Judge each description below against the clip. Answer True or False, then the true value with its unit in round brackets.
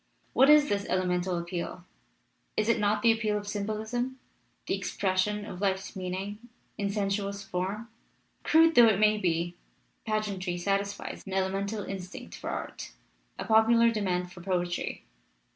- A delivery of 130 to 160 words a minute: True (145 wpm)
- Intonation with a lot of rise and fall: False (2.6 semitones)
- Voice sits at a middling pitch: False (200 Hz)